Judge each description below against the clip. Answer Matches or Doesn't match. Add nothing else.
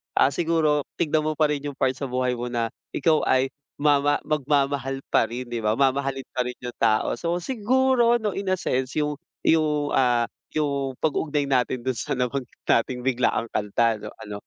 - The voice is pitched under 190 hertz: Matches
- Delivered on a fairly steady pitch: Doesn't match